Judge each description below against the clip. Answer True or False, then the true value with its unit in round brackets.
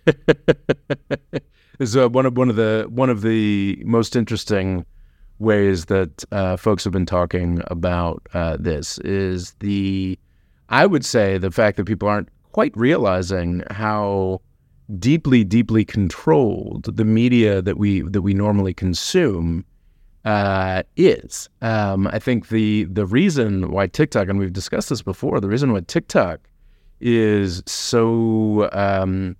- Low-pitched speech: True (100 Hz)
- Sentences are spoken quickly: False (140 wpm)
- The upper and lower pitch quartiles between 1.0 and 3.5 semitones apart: True (3.2 semitones)